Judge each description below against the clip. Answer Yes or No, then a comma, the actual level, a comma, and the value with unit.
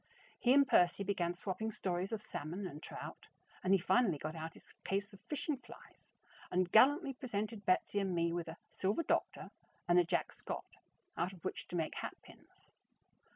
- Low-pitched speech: No, high, 190 Hz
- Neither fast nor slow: Yes, average, 180 wpm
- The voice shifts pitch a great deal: No, average, 4.0 semitones